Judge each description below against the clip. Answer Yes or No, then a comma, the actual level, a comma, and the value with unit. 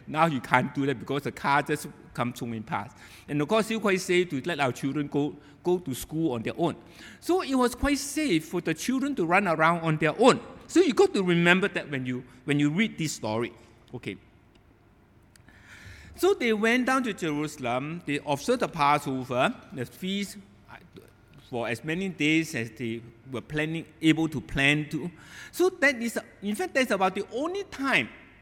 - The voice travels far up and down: Yes, wide, 7.5 semitones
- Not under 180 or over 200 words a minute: Yes, average, 195 wpm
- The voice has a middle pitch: Yes, medium, 155 Hz